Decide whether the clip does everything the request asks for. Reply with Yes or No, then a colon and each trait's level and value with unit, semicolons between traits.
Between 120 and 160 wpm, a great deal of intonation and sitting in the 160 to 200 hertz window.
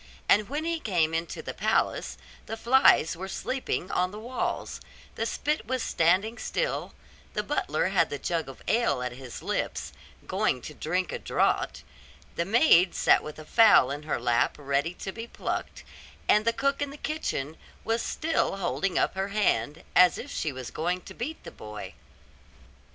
No: average, 180 wpm; wide, 7.1 semitones; medium, 185 Hz